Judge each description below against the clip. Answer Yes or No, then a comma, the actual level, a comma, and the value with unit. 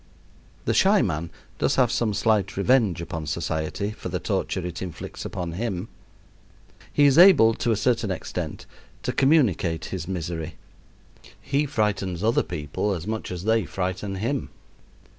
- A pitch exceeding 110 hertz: No, low, 100 Hz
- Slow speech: No, average, 150 wpm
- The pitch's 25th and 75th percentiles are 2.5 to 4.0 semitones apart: No, average, 4.8 semitones